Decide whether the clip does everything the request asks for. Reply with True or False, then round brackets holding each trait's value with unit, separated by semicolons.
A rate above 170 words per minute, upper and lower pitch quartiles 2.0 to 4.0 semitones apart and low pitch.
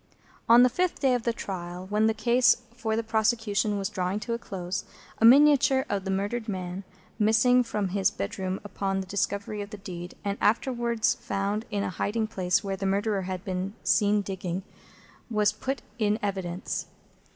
False (180 wpm; 2.8 semitones; 205 Hz)